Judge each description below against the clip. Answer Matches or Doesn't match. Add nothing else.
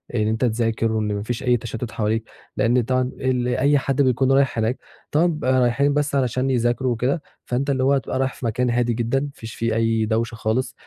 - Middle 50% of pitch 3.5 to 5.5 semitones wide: Doesn't match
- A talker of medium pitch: Doesn't match